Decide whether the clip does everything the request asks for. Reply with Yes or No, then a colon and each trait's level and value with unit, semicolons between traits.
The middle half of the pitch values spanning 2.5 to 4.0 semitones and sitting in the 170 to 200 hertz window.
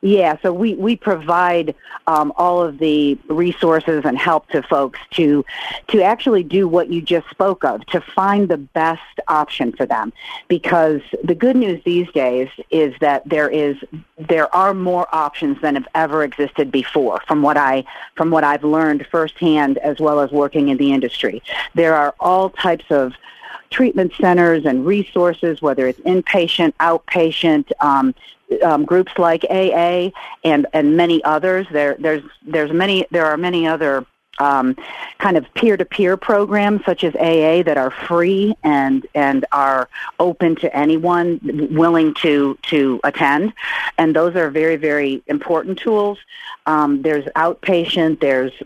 No: average, 3.3 semitones; medium, 160 Hz